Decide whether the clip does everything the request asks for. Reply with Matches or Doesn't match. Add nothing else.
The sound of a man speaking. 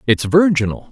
Matches